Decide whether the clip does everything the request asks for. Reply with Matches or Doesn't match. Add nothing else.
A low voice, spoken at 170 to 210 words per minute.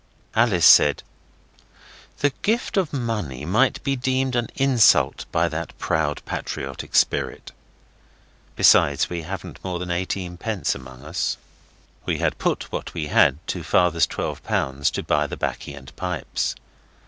Doesn't match